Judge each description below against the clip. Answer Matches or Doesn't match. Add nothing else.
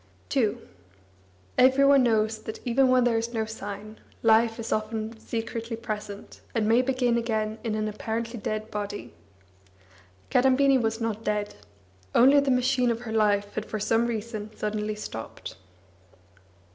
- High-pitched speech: Matches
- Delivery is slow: Doesn't match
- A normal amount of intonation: Doesn't match